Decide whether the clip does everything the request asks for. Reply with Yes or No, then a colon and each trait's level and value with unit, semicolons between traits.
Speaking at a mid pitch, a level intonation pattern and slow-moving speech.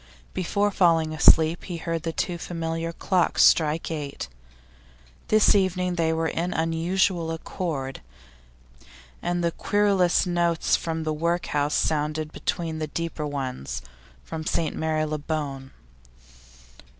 Yes: medium, 165 Hz; narrow, 2.0 semitones; slow, 115 wpm